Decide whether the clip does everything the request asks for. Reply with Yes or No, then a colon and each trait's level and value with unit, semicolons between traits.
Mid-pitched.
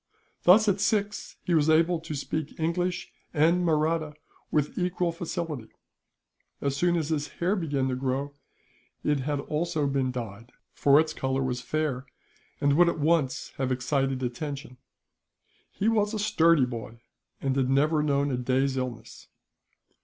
Yes: medium, 150 Hz